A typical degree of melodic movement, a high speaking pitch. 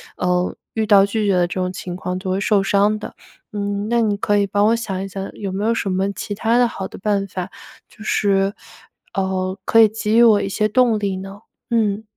No: narrow, 1.9 semitones; high, 200 Hz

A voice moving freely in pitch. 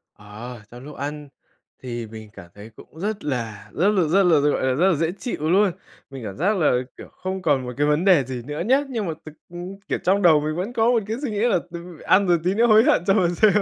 Yes: wide, 6.8 semitones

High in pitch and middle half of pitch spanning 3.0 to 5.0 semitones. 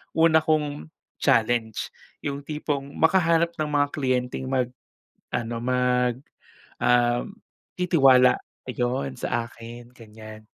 No: low, 125 Hz; average, 3.6 semitones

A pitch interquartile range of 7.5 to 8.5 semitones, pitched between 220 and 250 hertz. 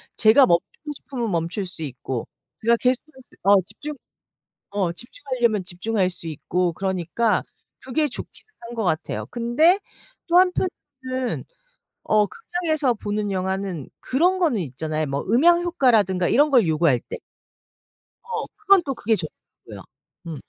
Yes: wide, 7.8 semitones; high, 225 Hz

